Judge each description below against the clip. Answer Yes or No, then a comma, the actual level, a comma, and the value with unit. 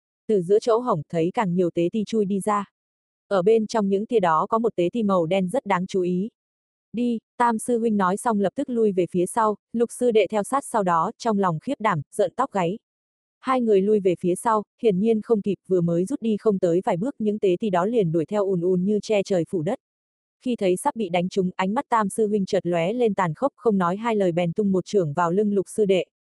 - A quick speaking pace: Yes, fast, 260 wpm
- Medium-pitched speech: No, high, 205 Hz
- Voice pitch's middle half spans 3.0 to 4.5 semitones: Yes, average, 3.8 semitones